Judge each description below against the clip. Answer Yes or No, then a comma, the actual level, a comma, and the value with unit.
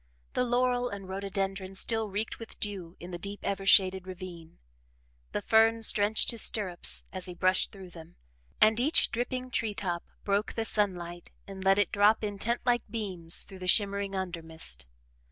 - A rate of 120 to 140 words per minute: No, average, 170 wpm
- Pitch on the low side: No, high, 200 Hz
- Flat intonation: No, average, 3.0 semitones